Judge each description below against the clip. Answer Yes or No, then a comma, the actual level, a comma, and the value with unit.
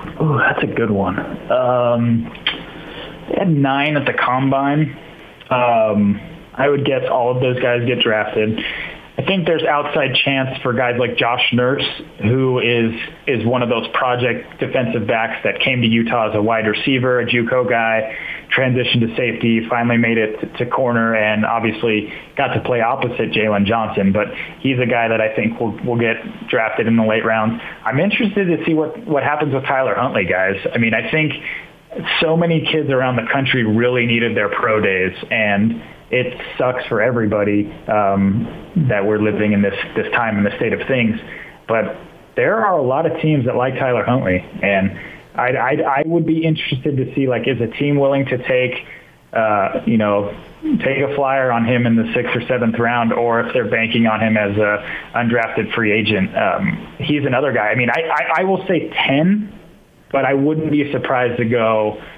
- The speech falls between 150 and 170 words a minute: No, average, 190 wpm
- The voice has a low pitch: Yes, low, 125 Hz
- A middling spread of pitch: Yes, average, 3.8 semitones